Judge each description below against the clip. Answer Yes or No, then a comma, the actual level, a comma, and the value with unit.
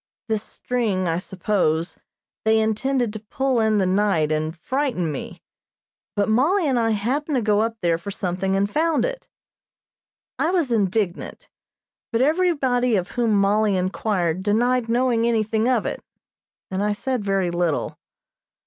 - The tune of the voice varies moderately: Yes, average, 4.6 semitones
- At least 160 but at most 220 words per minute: No, average, 150 wpm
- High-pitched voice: Yes, high, 215 Hz